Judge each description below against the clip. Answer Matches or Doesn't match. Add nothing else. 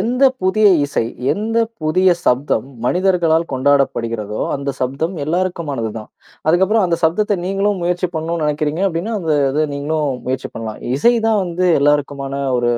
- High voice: Doesn't match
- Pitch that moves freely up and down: Doesn't match